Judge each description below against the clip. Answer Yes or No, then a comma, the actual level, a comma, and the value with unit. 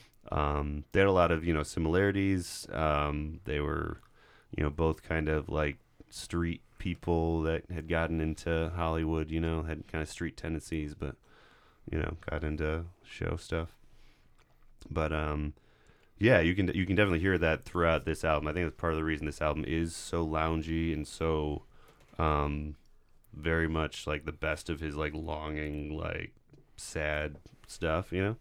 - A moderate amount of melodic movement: No, narrow, 1.8 semitones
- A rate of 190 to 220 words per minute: No, average, 170 wpm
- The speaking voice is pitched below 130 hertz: Yes, very low, 80 Hz